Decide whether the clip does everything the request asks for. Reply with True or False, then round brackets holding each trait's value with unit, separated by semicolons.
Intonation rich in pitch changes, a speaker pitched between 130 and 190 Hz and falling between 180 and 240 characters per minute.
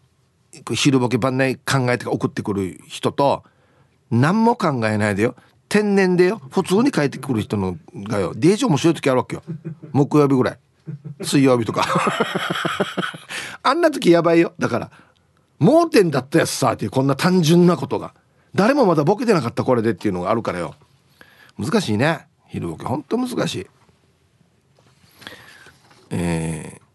False (5.9 semitones; 140 Hz; 295 characters per minute)